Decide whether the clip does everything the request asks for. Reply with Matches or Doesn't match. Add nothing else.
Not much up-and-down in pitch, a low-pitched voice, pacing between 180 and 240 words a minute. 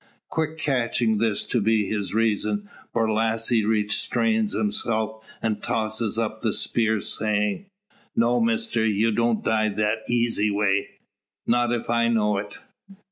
Doesn't match